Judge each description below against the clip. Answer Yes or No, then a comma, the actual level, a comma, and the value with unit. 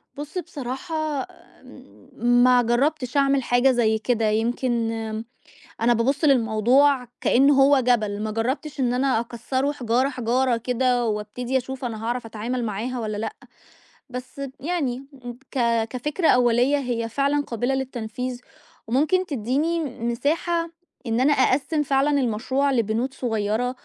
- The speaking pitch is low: No, very high, 250 Hz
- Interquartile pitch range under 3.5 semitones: Yes, average, 3.1 semitones